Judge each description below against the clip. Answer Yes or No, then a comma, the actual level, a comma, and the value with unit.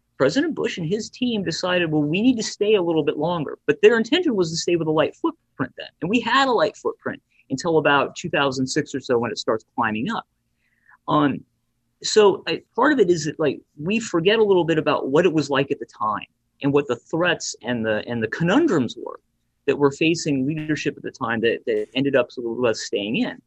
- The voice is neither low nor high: Yes, medium, 175 Hz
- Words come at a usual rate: No, fast, 225 wpm